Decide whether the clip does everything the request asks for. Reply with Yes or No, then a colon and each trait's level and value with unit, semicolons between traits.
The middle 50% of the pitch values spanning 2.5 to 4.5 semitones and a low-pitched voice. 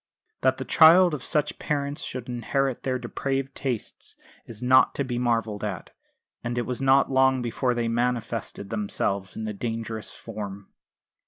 Yes: average, 3.1 semitones; low, 120 Hz